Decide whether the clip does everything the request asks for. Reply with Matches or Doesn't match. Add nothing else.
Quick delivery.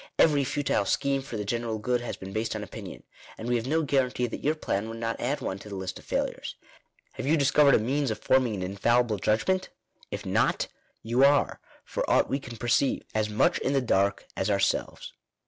Matches